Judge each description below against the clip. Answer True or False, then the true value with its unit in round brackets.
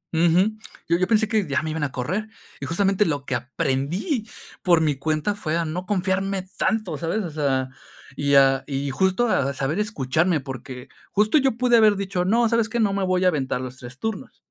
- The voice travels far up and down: True (6.9 semitones)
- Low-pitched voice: False (175 Hz)